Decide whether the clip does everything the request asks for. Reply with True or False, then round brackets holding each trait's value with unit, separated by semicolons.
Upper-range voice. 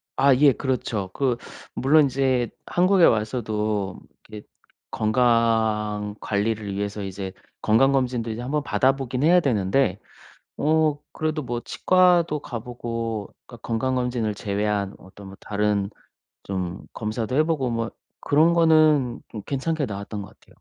False (120 Hz)